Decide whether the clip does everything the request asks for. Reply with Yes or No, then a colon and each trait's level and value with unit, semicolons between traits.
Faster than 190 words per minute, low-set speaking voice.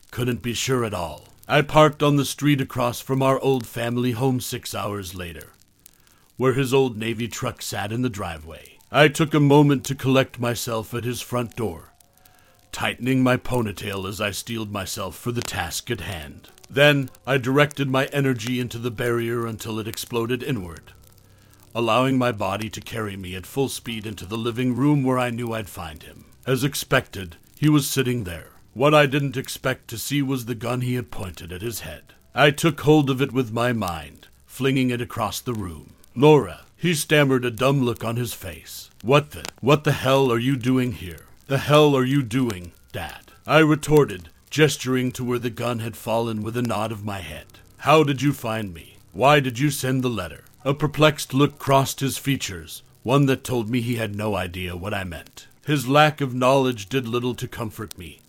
Yes: average, 200 wpm; low, 120 Hz